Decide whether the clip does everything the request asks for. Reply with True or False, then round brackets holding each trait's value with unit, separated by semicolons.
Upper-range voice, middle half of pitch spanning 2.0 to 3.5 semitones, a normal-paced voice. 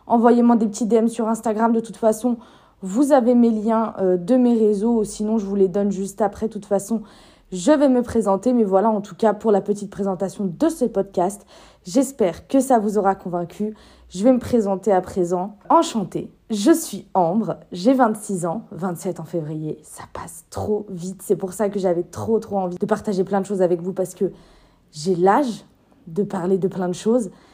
True (205 Hz; 3.2 semitones; 205 wpm)